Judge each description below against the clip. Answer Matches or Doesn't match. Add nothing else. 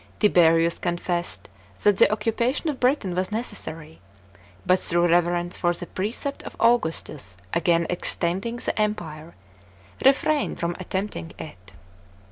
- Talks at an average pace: Doesn't match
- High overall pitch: Doesn't match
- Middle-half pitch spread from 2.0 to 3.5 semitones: Doesn't match